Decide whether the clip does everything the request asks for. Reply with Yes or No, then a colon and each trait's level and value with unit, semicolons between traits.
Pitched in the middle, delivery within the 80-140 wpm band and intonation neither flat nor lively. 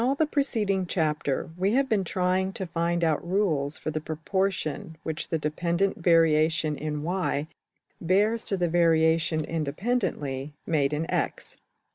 Yes: medium, 165 Hz; slow, 135 wpm; average, 3.7 semitones